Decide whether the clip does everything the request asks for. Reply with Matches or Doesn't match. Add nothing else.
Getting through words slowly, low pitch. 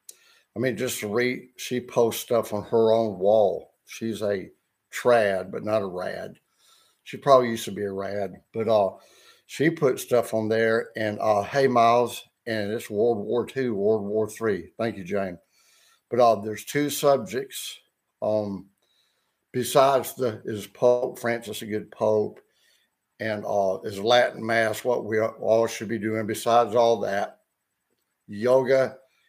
Doesn't match